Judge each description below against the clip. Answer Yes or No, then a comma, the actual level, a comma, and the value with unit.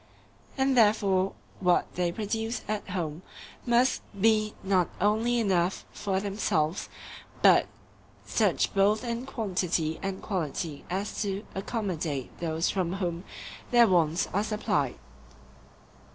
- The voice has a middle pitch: No, high, 195 Hz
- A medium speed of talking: No, slow, 115 wpm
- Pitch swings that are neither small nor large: Yes, average, 3.7 semitones